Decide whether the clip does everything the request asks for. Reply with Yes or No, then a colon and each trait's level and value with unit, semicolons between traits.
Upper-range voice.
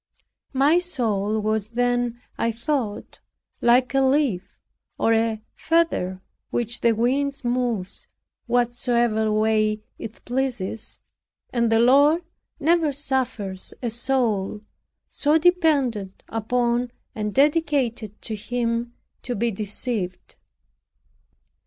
Yes: high, 235 Hz